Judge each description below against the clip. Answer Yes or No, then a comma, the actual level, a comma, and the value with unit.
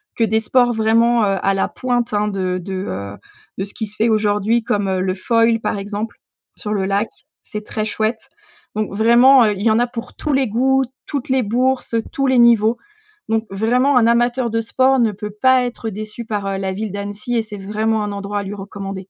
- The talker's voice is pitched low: No, high, 220 Hz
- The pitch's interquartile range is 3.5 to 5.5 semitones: No, average, 2.8 semitones